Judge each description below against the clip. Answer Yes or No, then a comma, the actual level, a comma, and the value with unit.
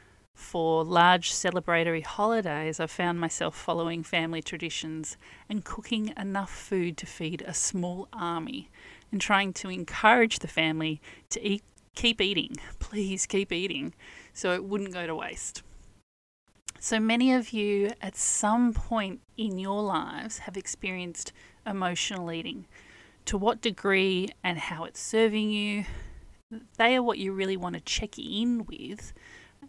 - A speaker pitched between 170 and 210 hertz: Yes, high, 190 Hz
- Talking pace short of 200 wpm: Yes, average, 140 wpm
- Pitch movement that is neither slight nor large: Yes, average, 4.2 semitones